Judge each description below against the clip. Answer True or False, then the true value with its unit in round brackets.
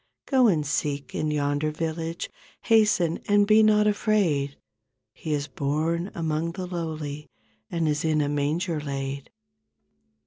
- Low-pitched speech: False (160 Hz)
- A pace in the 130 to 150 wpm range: True (135 wpm)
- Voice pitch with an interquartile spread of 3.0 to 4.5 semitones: True (3.6 semitones)